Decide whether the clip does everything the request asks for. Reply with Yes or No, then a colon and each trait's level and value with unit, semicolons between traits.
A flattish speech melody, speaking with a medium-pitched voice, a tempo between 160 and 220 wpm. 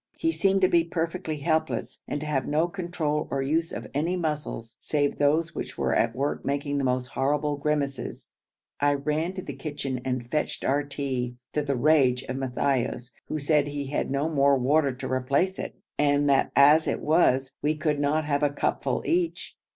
Yes: narrow, 2.3 semitones; medium, 145 Hz; average, 190 wpm